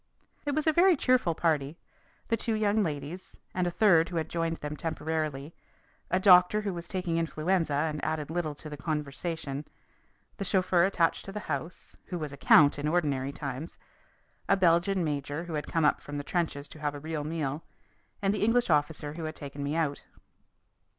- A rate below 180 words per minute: No, average, 190 wpm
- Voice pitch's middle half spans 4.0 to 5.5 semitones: No, average, 3.6 semitones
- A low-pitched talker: No, medium, 160 Hz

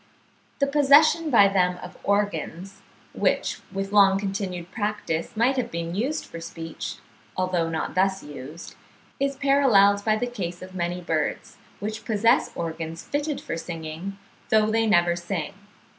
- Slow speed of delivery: No, average, 145 wpm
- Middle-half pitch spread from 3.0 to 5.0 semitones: Yes, average, 4.4 semitones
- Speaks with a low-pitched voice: No, high, 195 Hz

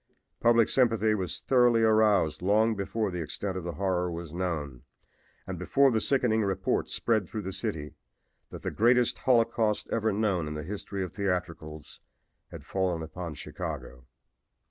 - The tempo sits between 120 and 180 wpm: Yes, average, 155 wpm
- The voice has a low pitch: Yes, very low, 95 Hz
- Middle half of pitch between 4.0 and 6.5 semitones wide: Yes, average, 4.5 semitones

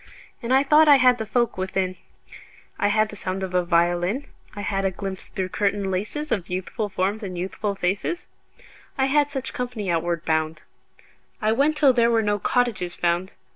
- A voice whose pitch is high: Yes, high, 205 Hz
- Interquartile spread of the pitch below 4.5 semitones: No, average, 5.0 semitones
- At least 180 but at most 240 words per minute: Yes, average, 185 wpm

